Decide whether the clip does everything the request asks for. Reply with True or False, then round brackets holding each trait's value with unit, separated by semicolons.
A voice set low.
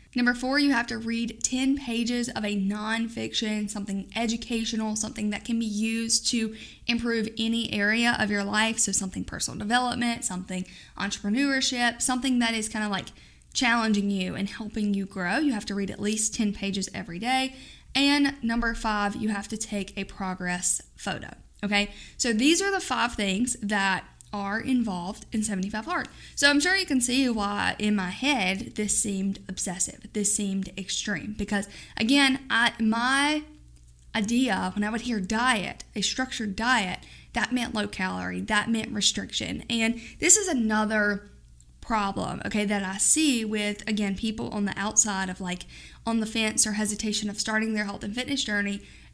False (215 Hz)